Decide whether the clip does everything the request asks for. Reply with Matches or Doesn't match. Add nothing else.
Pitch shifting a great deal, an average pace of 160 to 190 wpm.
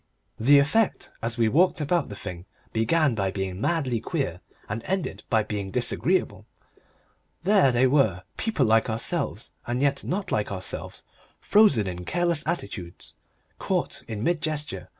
Doesn't match